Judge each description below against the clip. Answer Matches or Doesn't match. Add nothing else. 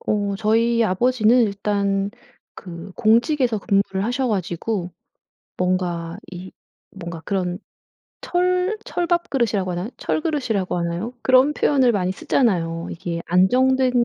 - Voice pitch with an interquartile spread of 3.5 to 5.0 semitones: Doesn't match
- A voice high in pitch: Matches